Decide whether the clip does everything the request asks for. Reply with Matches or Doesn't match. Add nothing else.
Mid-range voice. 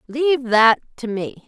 Doesn't match